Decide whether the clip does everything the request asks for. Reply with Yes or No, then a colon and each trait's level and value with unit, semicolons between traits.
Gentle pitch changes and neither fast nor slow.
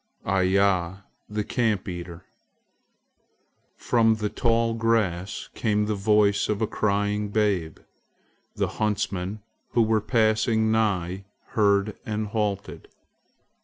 No: narrow, 2.0 semitones; slow, 105 wpm